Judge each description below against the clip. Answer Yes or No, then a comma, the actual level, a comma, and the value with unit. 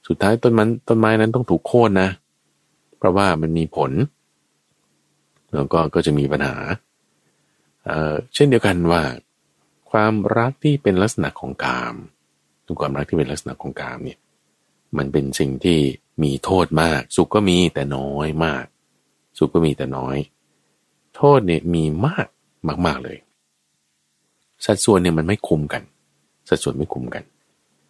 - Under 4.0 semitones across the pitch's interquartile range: No, average, 5.3 semitones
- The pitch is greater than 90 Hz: No, very low, 80 Hz